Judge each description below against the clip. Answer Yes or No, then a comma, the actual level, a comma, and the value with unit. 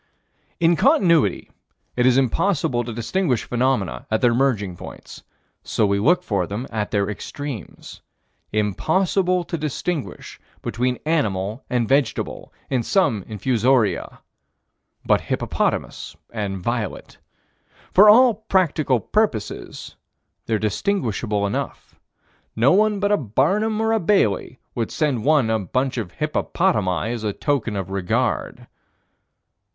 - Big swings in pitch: Yes, wide, 7.8 semitones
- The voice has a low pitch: Yes, low, 125 Hz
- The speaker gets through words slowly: Yes, slow, 125 wpm